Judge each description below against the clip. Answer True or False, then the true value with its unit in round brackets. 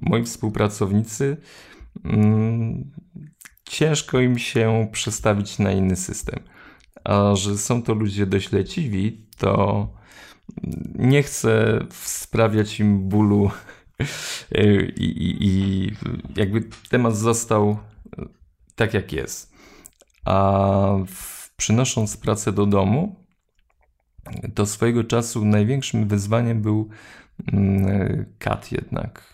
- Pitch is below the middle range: True (105 Hz)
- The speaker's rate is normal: False (90 wpm)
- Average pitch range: False (2.3 semitones)